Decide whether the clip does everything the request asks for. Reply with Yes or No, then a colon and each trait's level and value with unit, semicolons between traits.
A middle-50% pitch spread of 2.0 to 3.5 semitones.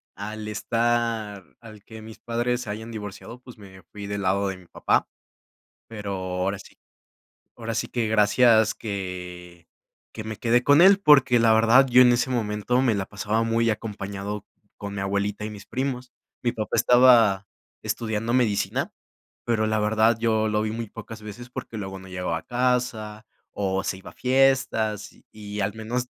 Yes: average, 2.7 semitones